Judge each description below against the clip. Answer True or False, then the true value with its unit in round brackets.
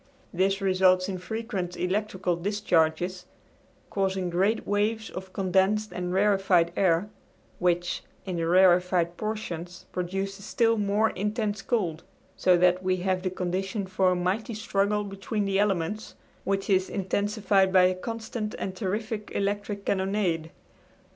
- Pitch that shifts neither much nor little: False (2.3 semitones)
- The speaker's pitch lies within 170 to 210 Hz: True (190 Hz)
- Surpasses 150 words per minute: False (135 wpm)